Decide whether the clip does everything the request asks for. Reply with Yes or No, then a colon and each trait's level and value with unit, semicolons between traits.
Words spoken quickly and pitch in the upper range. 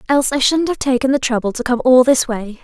Yes: fast, 275 wpm; very high, 255 Hz